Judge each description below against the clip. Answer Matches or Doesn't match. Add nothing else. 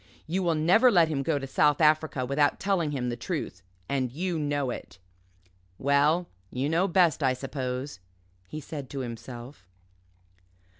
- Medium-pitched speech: Matches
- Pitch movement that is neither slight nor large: Matches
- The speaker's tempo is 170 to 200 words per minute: Doesn't match